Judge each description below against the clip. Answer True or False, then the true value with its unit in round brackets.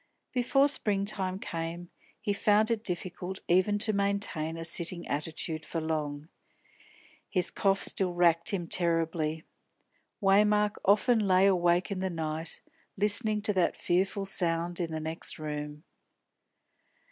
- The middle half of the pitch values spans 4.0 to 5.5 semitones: False (3.5 semitones)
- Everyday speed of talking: False (130 wpm)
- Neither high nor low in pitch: True (180 Hz)